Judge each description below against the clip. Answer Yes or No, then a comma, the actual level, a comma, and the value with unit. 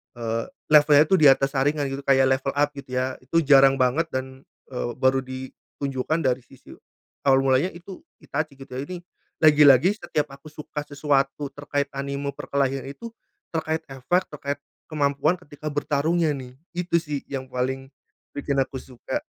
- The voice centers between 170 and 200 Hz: No, medium, 140 Hz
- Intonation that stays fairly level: Yes, narrow, 2.2 semitones